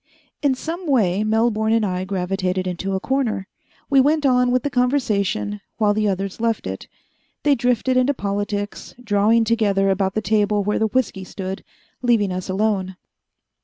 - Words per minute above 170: No, average, 165 wpm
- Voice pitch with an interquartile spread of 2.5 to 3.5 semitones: No, average, 4.1 semitones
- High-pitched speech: Yes, high, 210 Hz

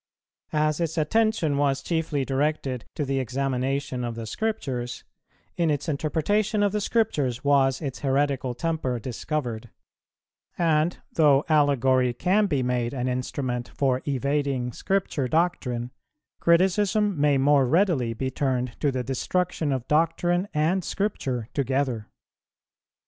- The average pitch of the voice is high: No, medium, 140 Hz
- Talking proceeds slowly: Yes, slow, 125 wpm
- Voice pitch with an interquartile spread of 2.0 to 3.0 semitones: No, average, 4.3 semitones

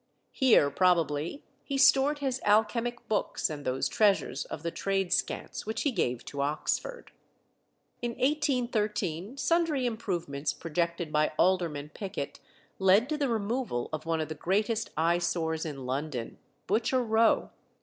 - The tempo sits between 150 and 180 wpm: No, average, 140 wpm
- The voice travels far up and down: Yes, wide, 7.3 semitones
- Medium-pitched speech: No, high, 195 Hz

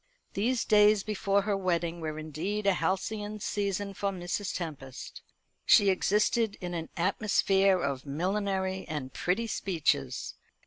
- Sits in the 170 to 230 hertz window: Yes, high, 190 Hz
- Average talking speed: No, slow, 130 wpm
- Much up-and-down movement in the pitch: No, average, 3.5 semitones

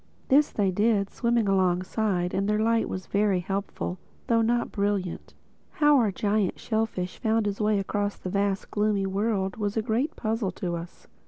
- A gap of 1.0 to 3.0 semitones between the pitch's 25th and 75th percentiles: Yes, narrow, 2.5 semitones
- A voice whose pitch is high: Yes, high, 205 Hz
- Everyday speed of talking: Yes, average, 175 wpm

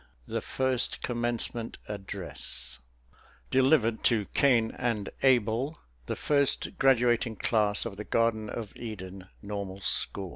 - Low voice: Yes, low, 115 Hz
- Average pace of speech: No, slow, 115 wpm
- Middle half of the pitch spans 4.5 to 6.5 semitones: No, average, 3.3 semitones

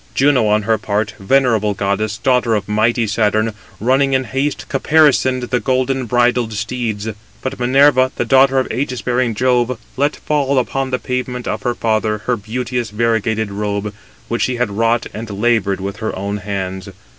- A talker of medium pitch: No, low, 120 Hz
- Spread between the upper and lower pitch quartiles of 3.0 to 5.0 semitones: Yes, average, 3.3 semitones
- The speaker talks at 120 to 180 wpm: Yes, average, 170 wpm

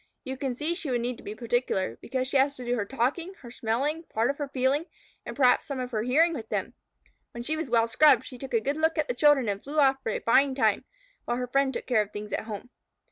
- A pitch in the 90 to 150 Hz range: No, very high, 255 Hz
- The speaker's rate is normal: No, fast, 270 wpm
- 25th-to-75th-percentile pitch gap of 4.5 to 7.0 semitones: No, average, 3.2 semitones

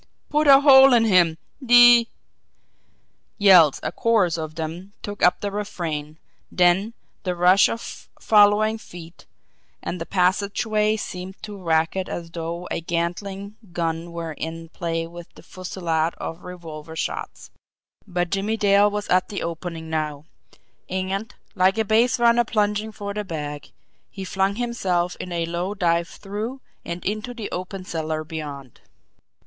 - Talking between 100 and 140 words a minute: No, average, 150 wpm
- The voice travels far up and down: No, average, 3.8 semitones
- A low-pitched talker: No, medium, 185 Hz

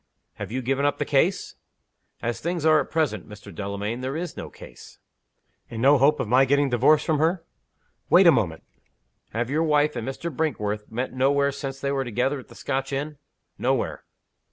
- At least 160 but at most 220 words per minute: Yes, average, 190 wpm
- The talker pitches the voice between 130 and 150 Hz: Yes, low, 135 Hz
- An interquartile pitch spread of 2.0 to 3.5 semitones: No, average, 3.9 semitones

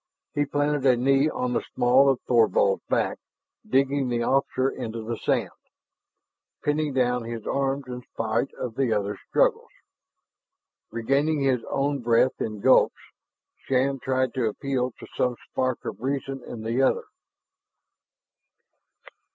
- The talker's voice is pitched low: Yes, low, 130 Hz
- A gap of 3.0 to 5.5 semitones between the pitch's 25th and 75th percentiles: No, narrow, 2.6 semitones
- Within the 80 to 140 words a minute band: Yes, slow, 135 wpm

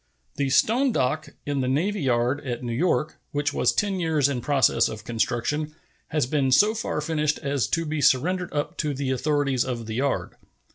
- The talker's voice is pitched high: No, medium, 145 Hz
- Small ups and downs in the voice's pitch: No, average, 3.3 semitones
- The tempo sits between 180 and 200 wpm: Yes, average, 190 wpm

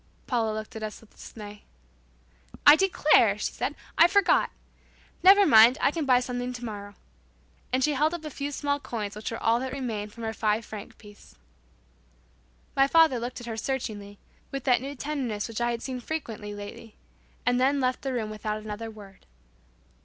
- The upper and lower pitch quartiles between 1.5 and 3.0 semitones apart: No, average, 4.3 semitones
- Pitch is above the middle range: Yes, high, 240 Hz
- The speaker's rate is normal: Yes, average, 185 wpm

